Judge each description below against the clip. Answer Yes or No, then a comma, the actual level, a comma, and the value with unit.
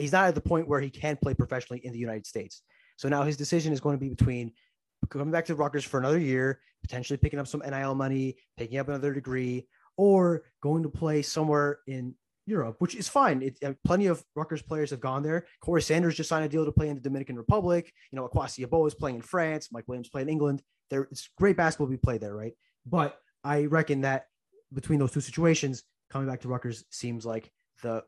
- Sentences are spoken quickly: Yes, fast, 230 wpm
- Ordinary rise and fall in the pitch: Yes, average, 3.6 semitones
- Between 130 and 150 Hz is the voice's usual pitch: Yes, medium, 140 Hz